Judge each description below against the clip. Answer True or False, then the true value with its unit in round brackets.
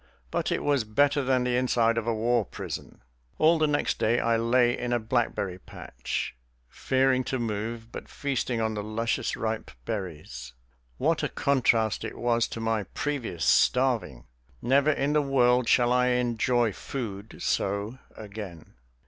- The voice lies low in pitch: True (120 Hz)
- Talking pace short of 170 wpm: True (155 wpm)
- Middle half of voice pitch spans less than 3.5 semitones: True (2.8 semitones)